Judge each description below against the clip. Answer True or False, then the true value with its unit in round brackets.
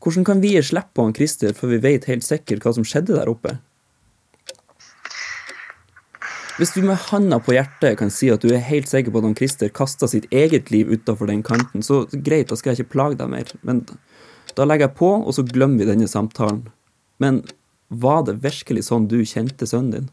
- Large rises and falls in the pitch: False (4.5 semitones)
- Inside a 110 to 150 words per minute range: False (200 wpm)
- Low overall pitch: True (130 Hz)